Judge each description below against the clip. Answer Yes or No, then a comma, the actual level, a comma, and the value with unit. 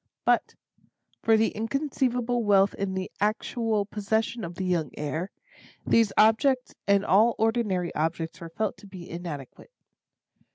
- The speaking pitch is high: Yes, high, 205 Hz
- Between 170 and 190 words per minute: No, slow, 135 wpm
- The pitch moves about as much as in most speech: Yes, average, 4.1 semitones